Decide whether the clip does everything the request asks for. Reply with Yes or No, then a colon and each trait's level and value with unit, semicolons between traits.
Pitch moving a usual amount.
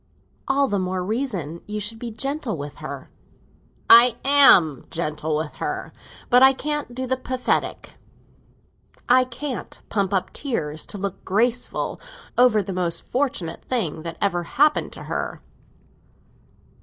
No: wide, 6.8 semitones